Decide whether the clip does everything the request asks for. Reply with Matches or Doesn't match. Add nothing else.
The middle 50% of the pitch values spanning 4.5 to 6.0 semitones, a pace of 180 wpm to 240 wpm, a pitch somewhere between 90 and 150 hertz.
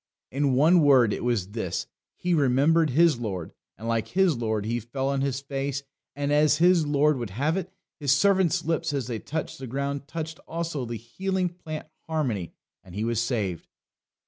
Matches